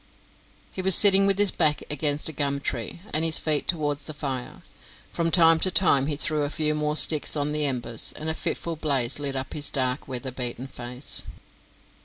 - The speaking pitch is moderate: Yes, medium, 150 Hz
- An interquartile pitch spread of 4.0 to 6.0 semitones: No, average, 2.8 semitones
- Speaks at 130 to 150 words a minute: No, average, 195 wpm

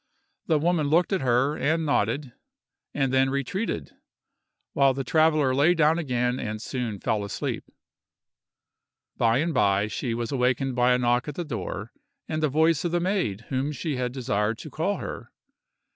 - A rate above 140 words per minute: Yes, average, 170 wpm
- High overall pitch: No, low, 135 Hz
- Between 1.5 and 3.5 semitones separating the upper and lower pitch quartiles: No, average, 4.5 semitones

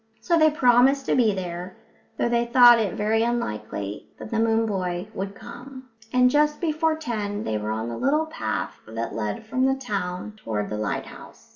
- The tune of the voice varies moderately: No, wide, 6.4 semitones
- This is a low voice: No, high, 225 Hz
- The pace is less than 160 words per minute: No, average, 185 wpm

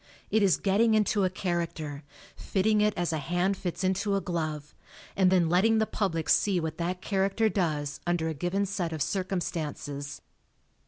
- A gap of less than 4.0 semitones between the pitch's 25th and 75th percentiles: Yes, average, 3.5 semitones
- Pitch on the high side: No, medium, 180 Hz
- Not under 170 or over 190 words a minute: Yes, average, 175 wpm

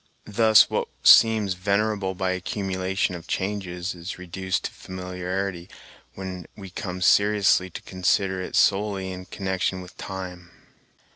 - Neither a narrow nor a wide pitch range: No, narrow, 1.4 semitones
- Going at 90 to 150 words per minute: Yes, slow, 135 wpm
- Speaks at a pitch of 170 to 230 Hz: No, very low, 95 Hz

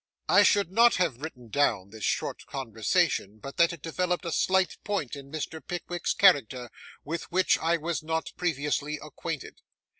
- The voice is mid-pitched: Yes, medium, 160 Hz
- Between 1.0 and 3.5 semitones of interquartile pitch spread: No, average, 4.3 semitones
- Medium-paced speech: Yes, average, 160 wpm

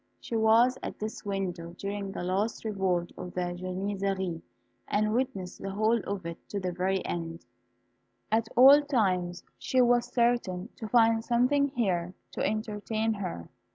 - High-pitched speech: Yes, high, 200 Hz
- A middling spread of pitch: Yes, average, 3.8 semitones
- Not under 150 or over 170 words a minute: Yes, average, 155 wpm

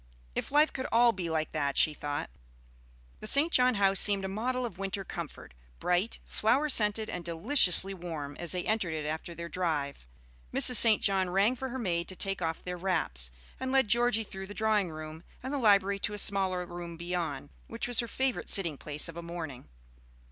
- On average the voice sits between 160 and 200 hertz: Yes, high, 190 Hz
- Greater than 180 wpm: Yes, average, 200 wpm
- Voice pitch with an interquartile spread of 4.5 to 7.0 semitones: Yes, average, 4.9 semitones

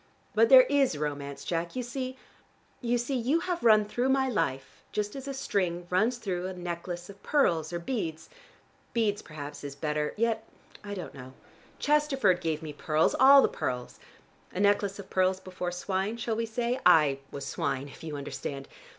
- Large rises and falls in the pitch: Yes, wide, 7.4 semitones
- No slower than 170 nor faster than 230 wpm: Yes, average, 180 wpm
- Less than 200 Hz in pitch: Yes, high, 190 Hz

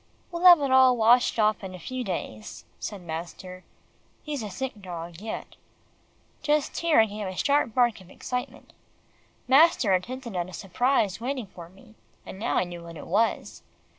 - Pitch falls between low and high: No, high, 215 Hz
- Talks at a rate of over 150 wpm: Yes, average, 180 wpm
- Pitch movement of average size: No, wide, 5.9 semitones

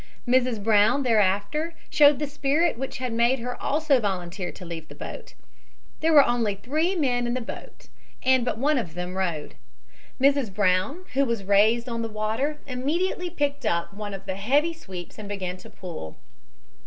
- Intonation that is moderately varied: No, wide, 6.0 semitones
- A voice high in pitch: Yes, high, 235 Hz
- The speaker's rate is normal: Yes, average, 180 wpm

